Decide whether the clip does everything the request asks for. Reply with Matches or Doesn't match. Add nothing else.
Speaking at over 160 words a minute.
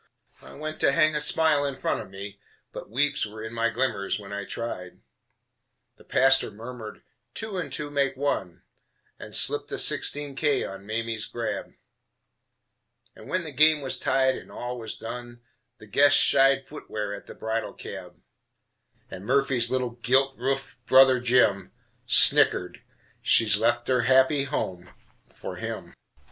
Doesn't match